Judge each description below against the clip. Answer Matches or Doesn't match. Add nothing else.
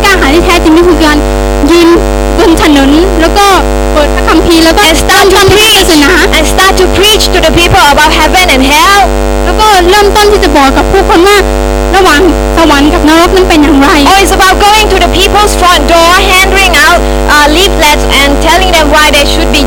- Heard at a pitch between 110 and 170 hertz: Doesn't match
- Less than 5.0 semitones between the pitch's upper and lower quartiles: Matches